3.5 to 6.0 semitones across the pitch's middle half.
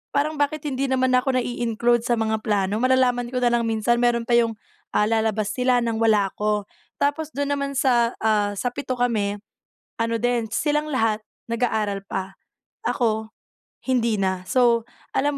No: average, 2.9 semitones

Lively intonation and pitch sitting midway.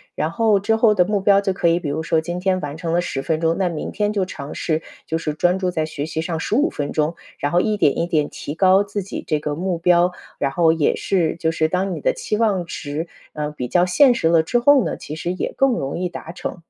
No: average, 3.5 semitones; medium, 175 Hz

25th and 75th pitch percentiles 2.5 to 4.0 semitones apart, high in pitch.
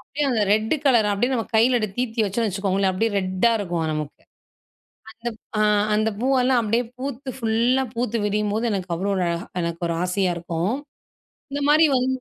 No: average, 4.6 semitones; high, 220 Hz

